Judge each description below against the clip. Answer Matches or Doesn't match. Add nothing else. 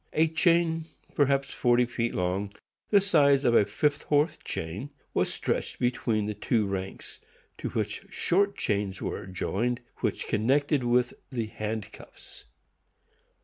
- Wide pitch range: Matches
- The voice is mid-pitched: Doesn't match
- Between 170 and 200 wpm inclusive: Doesn't match